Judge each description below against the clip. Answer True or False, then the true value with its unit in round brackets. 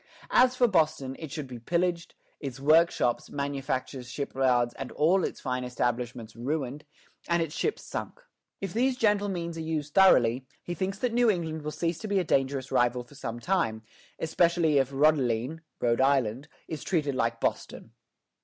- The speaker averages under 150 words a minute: False (165 wpm)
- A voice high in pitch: False (145 Hz)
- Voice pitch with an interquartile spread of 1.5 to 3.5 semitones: False (5.2 semitones)